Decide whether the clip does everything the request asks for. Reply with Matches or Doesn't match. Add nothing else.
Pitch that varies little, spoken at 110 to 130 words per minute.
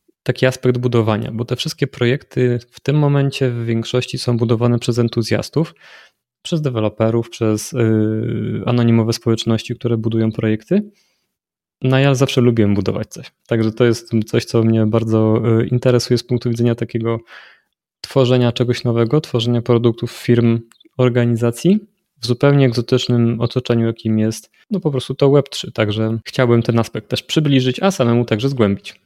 Doesn't match